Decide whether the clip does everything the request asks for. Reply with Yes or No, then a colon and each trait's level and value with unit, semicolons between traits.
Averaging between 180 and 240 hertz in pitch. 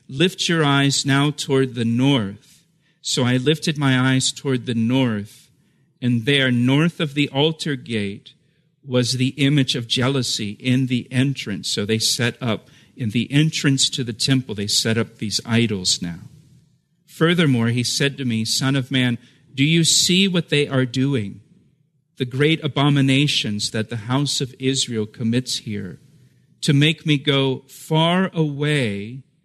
No: low, 135 Hz